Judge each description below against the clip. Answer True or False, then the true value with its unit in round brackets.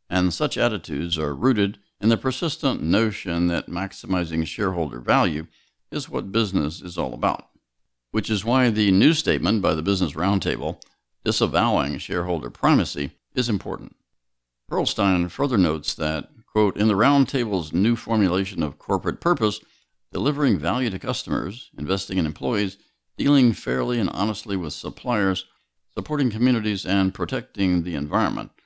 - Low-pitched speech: True (95 Hz)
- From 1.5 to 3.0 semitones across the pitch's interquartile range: False (4.5 semitones)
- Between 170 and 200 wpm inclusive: False (140 wpm)